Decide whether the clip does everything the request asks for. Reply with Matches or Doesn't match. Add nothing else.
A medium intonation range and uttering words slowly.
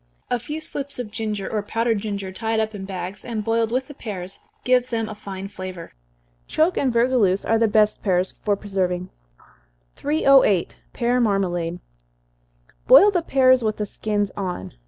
Doesn't match